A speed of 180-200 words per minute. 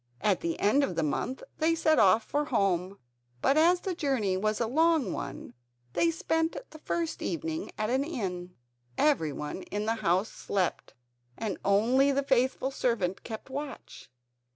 No: average, 160 wpm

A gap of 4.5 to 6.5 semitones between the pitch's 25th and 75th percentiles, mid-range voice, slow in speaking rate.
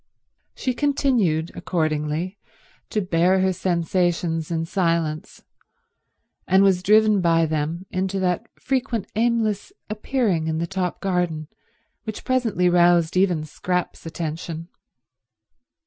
No: average, 3.3 semitones; medium, 180 Hz; slow, 110 wpm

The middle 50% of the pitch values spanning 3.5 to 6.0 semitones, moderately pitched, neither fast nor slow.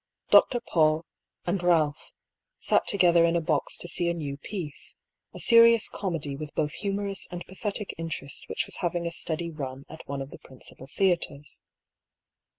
Yes: average, 4.0 semitones; medium, 170 Hz; average, 175 wpm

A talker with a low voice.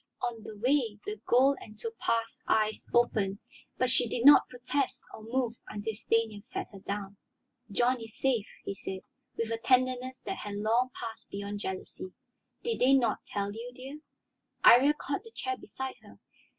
No: high, 230 Hz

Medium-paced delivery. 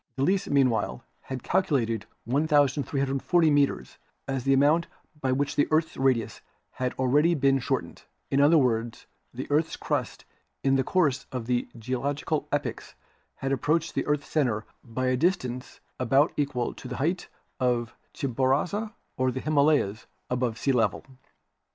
Yes: average, 145 wpm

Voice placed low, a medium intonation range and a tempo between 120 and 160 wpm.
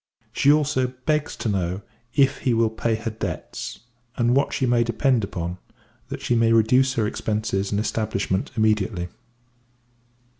Yes: low, 115 Hz; average, 3.5 semitones; average, 150 wpm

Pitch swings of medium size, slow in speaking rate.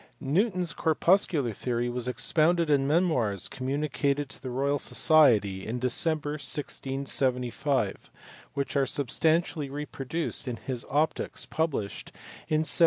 Yes: average, 3.8 semitones; slow, 120 wpm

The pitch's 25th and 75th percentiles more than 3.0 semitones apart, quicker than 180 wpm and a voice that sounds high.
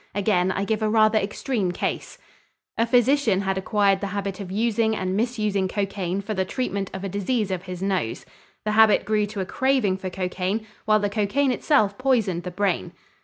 No: narrow, 2.6 semitones; average, 190 wpm; high, 200 Hz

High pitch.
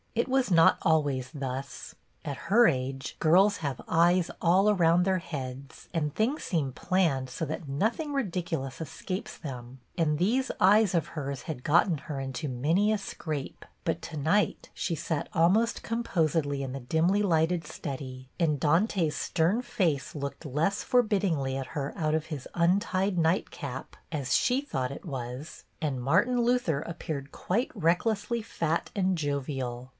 No: medium, 160 Hz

